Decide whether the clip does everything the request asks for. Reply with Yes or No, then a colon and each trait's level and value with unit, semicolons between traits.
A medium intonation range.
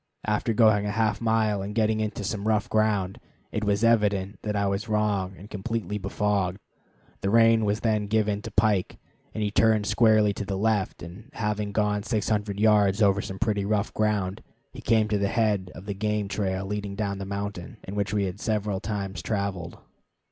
No: narrow, 1.5 semitones